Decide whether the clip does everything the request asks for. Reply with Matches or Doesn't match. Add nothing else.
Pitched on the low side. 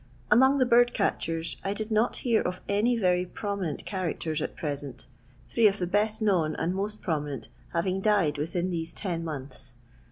Doesn't match